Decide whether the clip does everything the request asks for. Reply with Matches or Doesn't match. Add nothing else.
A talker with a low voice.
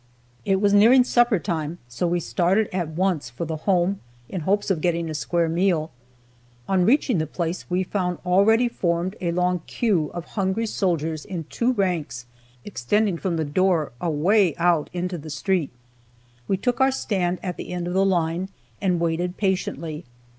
Doesn't match